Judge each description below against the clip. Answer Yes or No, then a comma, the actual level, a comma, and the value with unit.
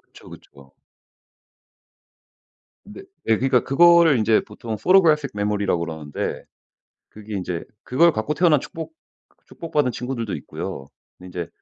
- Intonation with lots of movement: Yes, wide, 7.2 semitones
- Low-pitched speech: Yes, low, 120 Hz